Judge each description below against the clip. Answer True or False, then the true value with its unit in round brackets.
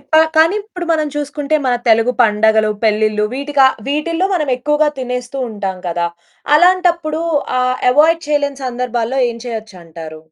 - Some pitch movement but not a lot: False (5.7 semitones)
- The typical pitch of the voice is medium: False (255 Hz)